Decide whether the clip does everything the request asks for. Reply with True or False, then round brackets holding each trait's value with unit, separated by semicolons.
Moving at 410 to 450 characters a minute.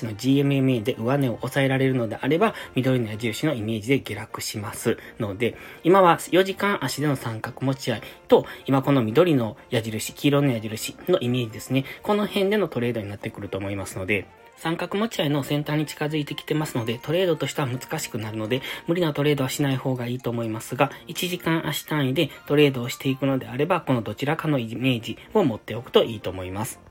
False (385 characters per minute)